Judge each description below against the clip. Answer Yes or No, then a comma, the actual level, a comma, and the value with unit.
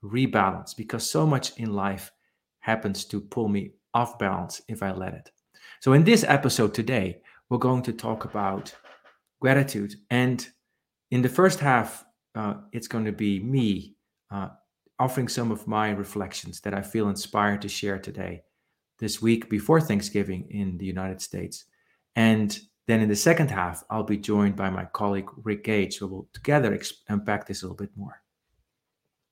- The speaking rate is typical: Yes, average, 170 wpm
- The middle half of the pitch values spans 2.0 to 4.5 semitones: Yes, average, 2.9 semitones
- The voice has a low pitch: Yes, low, 105 Hz